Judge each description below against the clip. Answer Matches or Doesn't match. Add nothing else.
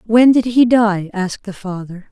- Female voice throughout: Matches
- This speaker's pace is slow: Doesn't match